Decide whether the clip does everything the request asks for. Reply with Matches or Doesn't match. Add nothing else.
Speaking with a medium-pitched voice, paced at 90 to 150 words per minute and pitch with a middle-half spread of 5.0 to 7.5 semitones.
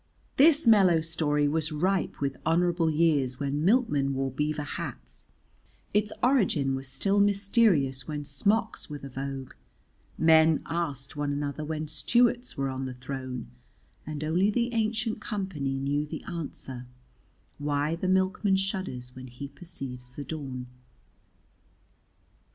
Matches